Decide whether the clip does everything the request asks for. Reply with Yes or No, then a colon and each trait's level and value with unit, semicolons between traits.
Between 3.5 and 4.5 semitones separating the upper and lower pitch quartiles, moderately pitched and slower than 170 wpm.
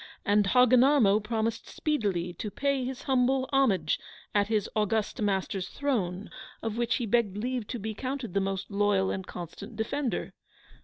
No: average, 4.2 semitones; high, 220 Hz; average, 155 wpm